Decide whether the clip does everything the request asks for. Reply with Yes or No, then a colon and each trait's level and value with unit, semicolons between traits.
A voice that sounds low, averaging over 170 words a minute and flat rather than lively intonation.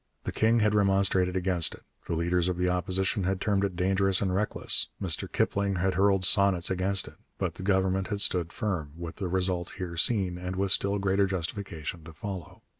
Yes: very low, 95 Hz; average, 195 wpm; narrow, 1.6 semitones